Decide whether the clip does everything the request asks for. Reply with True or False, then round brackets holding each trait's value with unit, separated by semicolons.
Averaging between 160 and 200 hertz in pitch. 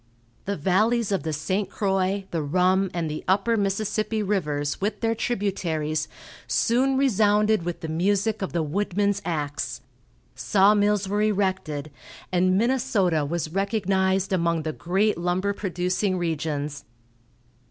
True (190 Hz)